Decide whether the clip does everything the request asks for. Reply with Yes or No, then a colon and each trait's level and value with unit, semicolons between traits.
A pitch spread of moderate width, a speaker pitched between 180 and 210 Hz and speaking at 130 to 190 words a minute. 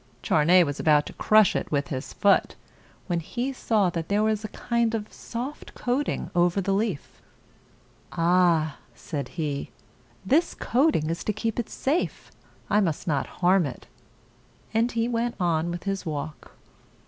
No: wide, 6.0 semitones; high, 190 Hz; average, 160 wpm